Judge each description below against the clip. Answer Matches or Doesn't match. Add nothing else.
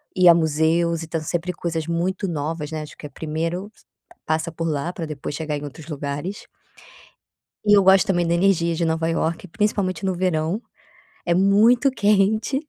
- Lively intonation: Doesn't match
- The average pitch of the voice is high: Doesn't match